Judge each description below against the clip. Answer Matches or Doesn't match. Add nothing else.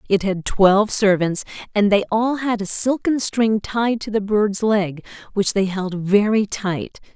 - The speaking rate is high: Doesn't match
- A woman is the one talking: Matches